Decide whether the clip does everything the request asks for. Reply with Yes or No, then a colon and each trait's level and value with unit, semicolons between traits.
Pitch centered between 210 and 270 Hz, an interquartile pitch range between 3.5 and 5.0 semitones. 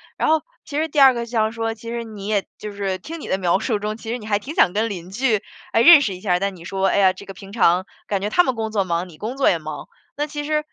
Yes: high, 215 Hz; average, 3.9 semitones